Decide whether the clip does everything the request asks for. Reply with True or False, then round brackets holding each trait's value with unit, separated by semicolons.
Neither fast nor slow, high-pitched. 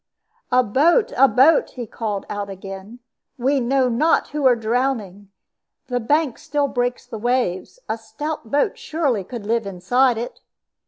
True (155 wpm; 245 Hz)